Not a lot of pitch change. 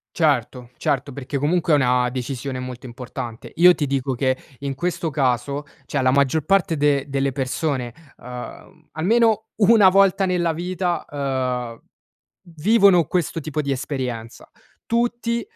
No: wide, 5.4 semitones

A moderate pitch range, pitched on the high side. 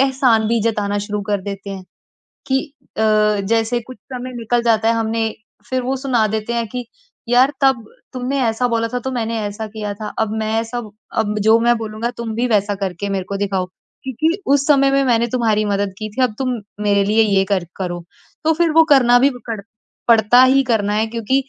Yes: average, 3.2 semitones; high, 225 Hz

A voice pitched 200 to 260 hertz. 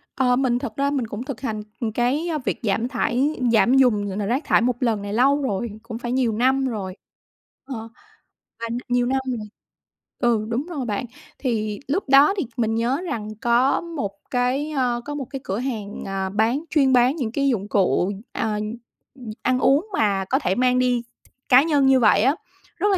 Yes: high, 245 Hz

